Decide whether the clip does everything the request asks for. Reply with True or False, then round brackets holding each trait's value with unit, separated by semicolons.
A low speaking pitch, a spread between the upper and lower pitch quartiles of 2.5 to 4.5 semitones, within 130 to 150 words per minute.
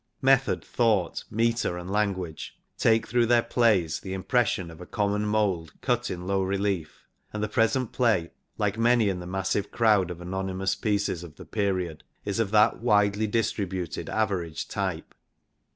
False (100 Hz; 3.3 semitones; 165 wpm)